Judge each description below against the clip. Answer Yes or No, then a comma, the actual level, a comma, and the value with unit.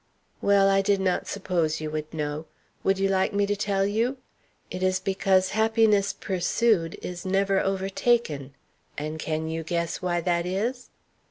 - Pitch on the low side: No, high, 190 Hz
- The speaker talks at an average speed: Yes, average, 160 wpm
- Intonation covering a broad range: No, average, 3.2 semitones